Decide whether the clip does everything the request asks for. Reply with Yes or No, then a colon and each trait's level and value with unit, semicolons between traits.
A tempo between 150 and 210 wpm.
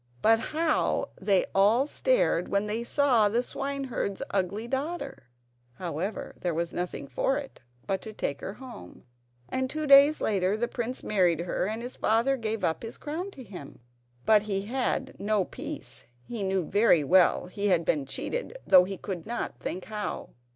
Yes: average, 170 wpm